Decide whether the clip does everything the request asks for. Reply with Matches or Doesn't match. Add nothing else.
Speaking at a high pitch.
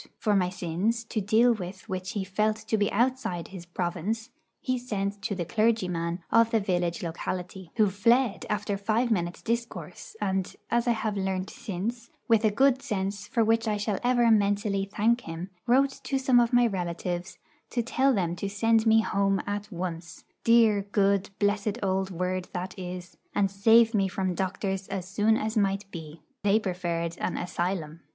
Matches